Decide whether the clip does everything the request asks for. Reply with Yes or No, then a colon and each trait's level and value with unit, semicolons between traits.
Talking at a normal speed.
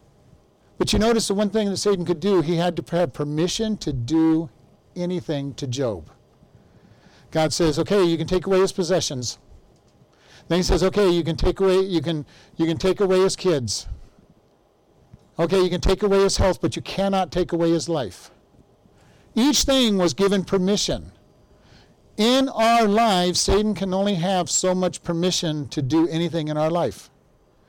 Yes: average, 175 wpm